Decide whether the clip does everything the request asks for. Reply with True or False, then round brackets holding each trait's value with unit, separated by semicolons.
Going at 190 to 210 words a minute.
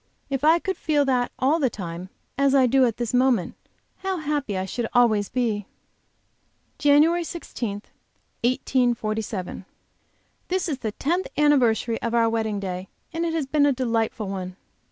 False (155 wpm)